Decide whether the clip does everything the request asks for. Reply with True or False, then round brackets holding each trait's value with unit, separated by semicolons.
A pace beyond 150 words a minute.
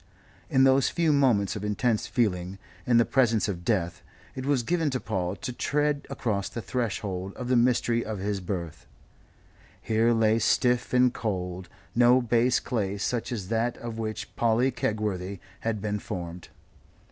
True (160 wpm)